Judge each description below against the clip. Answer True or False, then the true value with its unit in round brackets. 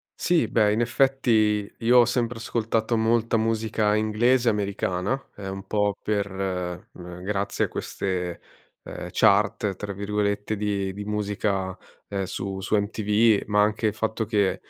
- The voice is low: True (105 Hz)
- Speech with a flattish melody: True (2.2 semitones)